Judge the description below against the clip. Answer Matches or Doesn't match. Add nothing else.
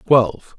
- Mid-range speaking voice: Doesn't match